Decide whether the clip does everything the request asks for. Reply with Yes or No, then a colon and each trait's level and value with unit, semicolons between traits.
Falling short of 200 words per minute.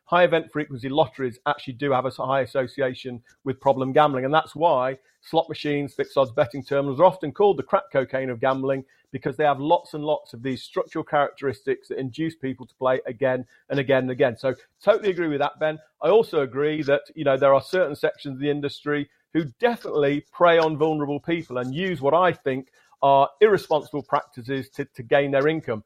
No: fast, 205 wpm